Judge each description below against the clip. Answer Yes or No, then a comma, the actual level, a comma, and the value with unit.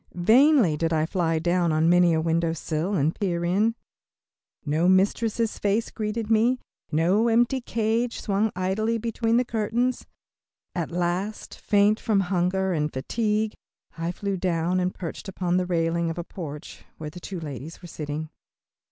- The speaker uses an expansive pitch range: No, average, 4.6 semitones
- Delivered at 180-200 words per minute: No, average, 155 wpm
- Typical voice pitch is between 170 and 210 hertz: Yes, medium, 185 Hz